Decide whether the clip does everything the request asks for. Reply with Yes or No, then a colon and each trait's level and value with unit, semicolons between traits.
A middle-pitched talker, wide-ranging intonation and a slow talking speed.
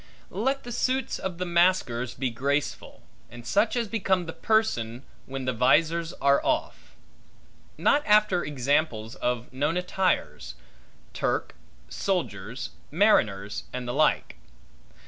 Yes: medium, 155 Hz; wide, 7.7 semitones; slow, 125 wpm